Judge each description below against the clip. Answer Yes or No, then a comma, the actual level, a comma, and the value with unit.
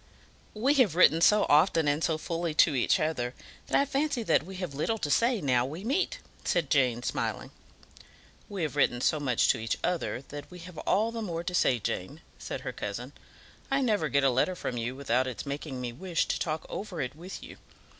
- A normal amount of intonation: No, wide, 5.9 semitones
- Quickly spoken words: Yes, fast, 215 wpm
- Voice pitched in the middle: Yes, medium, 160 Hz